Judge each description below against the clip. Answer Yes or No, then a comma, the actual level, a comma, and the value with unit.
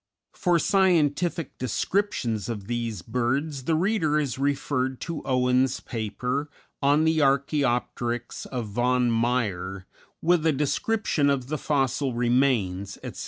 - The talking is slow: Yes, slow, 125 wpm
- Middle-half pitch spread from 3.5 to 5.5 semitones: Yes, average, 4.1 semitones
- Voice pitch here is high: No, low, 130 Hz